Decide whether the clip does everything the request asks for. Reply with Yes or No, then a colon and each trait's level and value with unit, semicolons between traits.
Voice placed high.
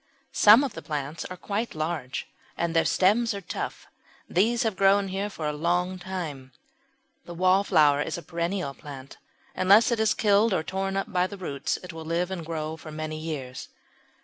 No: medium, 180 Hz